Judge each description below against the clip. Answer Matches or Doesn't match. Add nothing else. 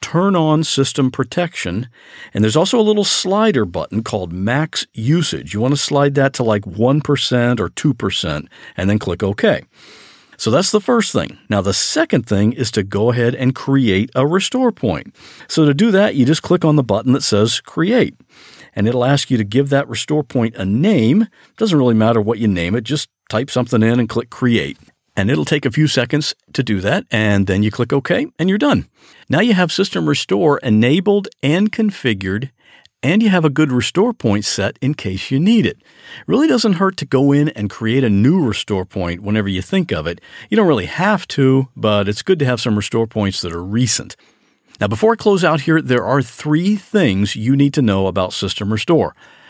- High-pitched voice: Doesn't match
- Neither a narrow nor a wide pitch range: Doesn't match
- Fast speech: Matches